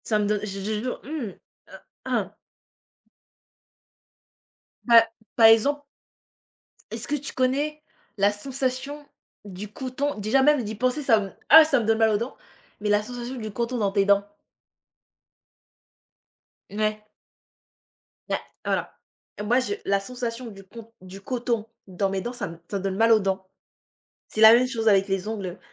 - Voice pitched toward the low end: No, high, 225 Hz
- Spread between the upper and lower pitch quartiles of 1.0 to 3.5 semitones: No, average, 3.9 semitones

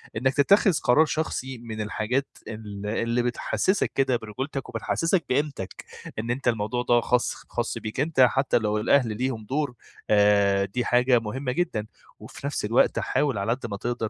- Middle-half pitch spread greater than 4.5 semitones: No, average, 3.8 semitones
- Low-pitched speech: Yes, low, 120 Hz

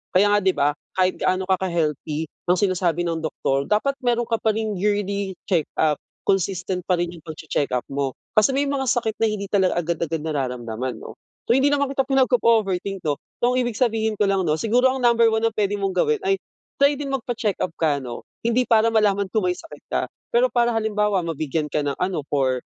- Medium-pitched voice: No, high, 195 Hz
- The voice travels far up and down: Yes, wide, 5.8 semitones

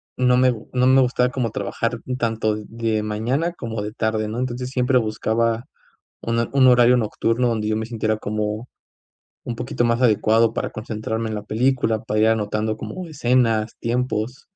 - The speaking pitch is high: No, low, 115 Hz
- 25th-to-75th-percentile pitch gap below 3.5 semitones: Yes, narrow, 2.4 semitones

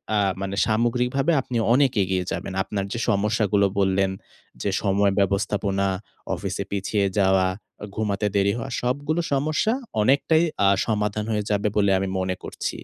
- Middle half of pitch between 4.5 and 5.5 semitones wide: No, average, 3.5 semitones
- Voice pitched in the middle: No, low, 105 Hz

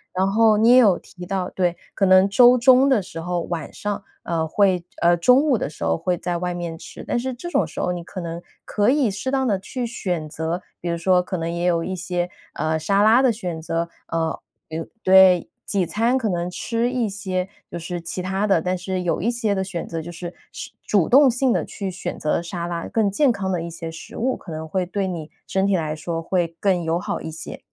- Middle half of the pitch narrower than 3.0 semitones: No, average, 3.8 semitones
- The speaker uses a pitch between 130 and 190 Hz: Yes, medium, 185 Hz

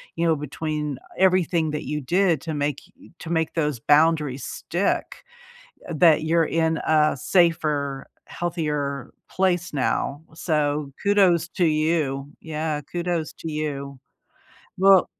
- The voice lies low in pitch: No, medium, 155 Hz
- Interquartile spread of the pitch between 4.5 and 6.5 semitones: No, narrow, 2.6 semitones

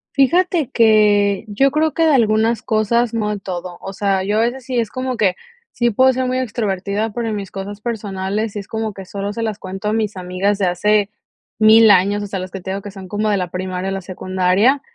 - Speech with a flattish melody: No, average, 3.0 semitones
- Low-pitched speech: No, high, 210 Hz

